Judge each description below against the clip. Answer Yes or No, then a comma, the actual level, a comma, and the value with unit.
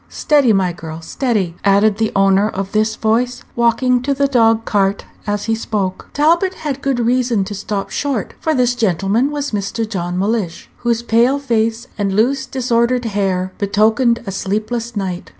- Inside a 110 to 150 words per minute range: No, average, 170 wpm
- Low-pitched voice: No, high, 225 Hz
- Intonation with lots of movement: No, average, 3.9 semitones